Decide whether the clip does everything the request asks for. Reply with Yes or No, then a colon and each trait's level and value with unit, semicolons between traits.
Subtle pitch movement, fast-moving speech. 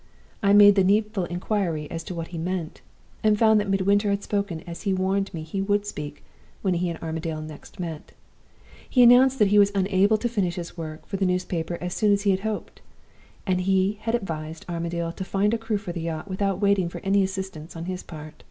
No: average, 3.2 semitones; fast, 225 wpm